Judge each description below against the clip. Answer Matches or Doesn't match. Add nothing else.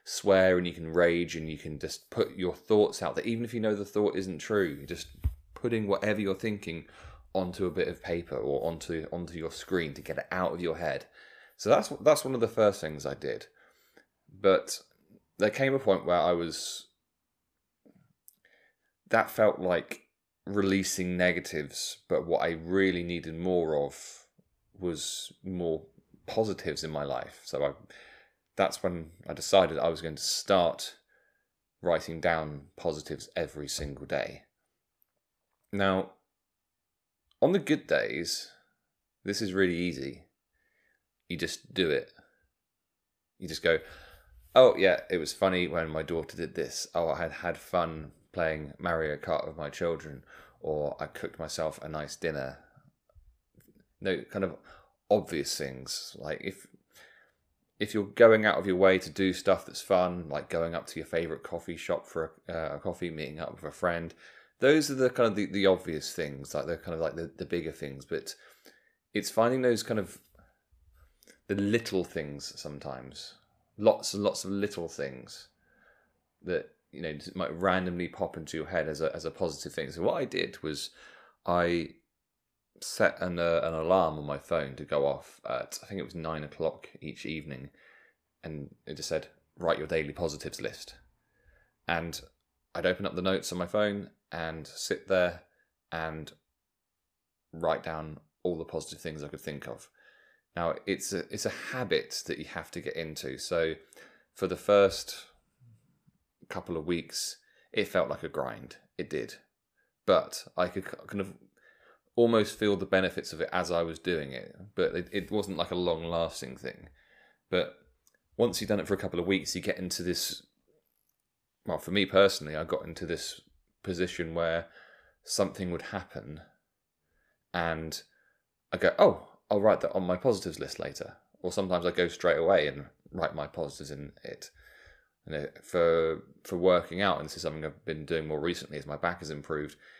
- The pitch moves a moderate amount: Matches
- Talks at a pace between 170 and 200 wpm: Matches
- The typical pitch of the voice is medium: Doesn't match